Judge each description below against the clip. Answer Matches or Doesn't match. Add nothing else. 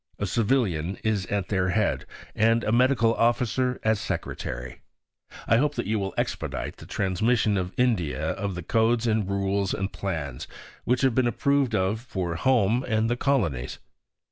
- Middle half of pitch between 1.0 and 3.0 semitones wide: Doesn't match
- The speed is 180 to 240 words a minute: Doesn't match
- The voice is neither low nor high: Doesn't match